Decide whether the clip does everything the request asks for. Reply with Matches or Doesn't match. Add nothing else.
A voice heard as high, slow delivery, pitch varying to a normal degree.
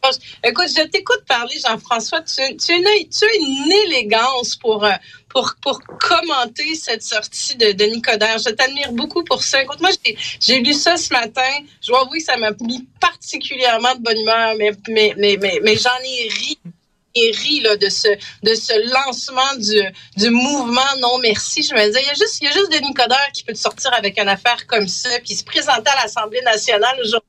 Doesn't match